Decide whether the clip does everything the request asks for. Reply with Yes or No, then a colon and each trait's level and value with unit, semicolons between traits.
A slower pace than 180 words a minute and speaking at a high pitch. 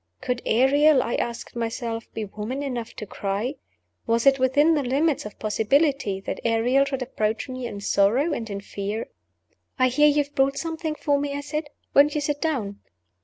No: average, 185 wpm; very high, 255 Hz